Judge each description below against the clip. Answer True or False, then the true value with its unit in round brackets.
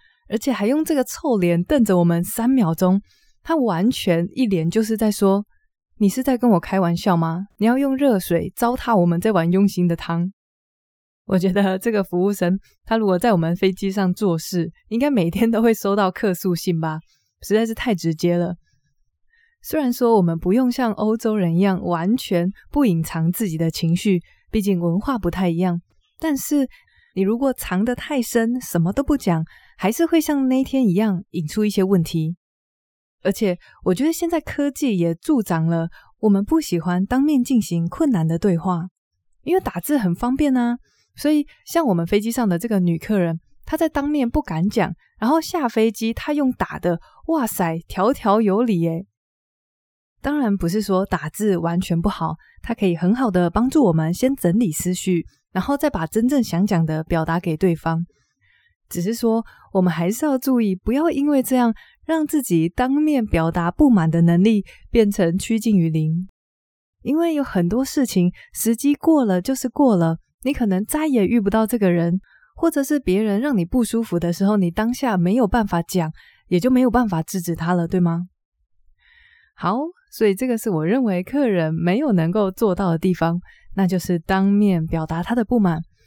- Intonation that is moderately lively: False (6.2 semitones)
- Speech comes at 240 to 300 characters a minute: True (265 characters per minute)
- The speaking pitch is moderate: False (200 Hz)